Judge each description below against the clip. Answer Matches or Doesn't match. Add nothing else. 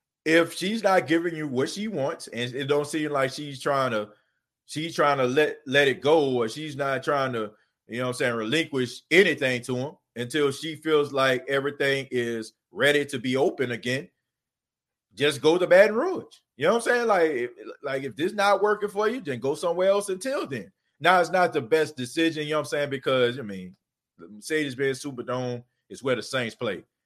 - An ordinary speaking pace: Doesn't match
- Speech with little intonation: Doesn't match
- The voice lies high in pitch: Doesn't match